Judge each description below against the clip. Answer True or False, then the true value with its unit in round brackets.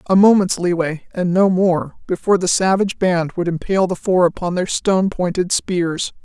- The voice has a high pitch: False (180 Hz)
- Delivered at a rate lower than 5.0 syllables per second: False (5.3 syllables/s)